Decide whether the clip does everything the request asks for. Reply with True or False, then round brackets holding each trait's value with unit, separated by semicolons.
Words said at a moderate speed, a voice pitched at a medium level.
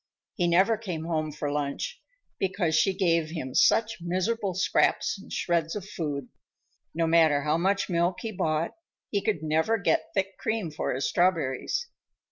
True (160 wpm; 170 Hz)